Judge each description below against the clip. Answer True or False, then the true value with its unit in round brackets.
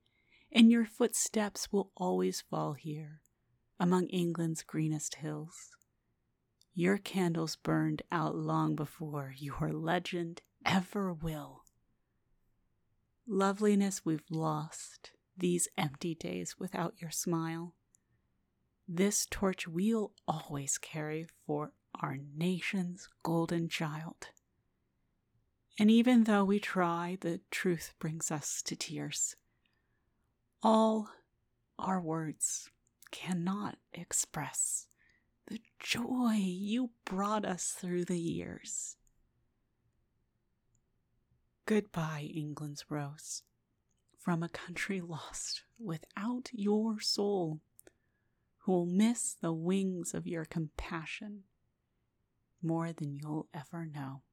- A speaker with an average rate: False (95 wpm)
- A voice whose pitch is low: False (170 Hz)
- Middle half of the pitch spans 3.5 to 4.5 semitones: True (4.1 semitones)